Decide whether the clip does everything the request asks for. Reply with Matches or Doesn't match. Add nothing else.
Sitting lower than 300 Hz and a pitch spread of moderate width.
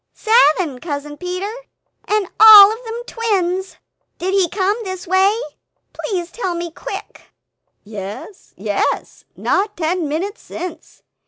Doesn't match